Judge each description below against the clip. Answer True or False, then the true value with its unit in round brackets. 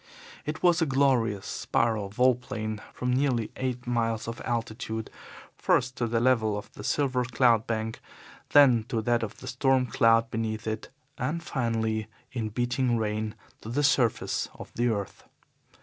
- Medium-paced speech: True (160 wpm)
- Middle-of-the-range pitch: False (115 Hz)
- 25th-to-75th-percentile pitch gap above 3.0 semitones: False (2.5 semitones)